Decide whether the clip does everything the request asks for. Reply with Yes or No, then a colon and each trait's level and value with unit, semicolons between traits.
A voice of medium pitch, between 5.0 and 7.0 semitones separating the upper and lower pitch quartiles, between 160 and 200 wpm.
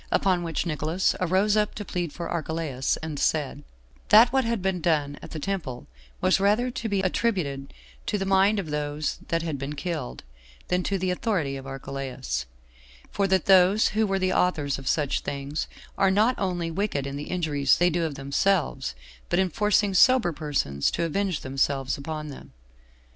Yes: medium, 170 Hz; average, 5.3 semitones; average, 180 wpm